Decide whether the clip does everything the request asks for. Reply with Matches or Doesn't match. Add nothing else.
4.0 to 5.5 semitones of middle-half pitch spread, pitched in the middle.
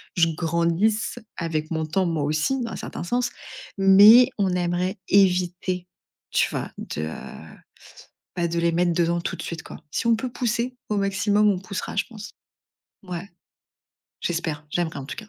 Doesn't match